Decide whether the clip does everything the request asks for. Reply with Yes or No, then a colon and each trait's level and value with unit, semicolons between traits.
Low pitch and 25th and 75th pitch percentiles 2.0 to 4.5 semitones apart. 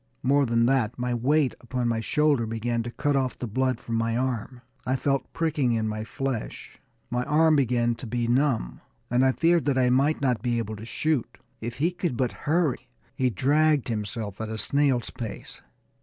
Yes: low, 125 Hz; average, 3.4 semitones